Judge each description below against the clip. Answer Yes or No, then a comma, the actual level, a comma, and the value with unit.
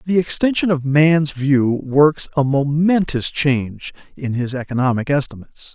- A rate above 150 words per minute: No, slow, 135 wpm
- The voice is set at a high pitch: No, medium, 145 Hz